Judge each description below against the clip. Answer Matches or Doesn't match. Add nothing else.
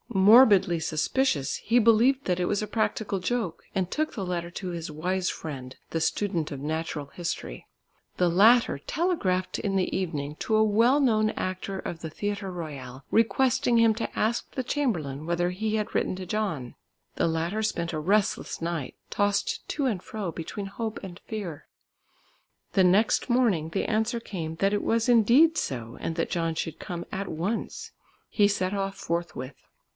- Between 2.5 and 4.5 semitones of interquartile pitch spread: Doesn't match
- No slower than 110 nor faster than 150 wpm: Doesn't match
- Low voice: Doesn't match